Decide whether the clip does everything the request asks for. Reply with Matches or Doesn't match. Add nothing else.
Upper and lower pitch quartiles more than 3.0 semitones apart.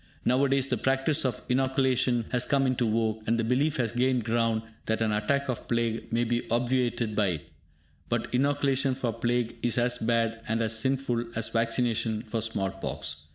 Doesn't match